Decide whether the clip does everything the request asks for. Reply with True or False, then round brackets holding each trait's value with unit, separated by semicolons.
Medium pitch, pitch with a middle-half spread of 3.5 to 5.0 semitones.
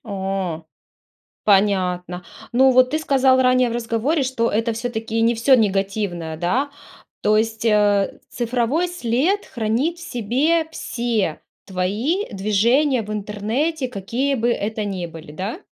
False (225 Hz; 4.5 semitones)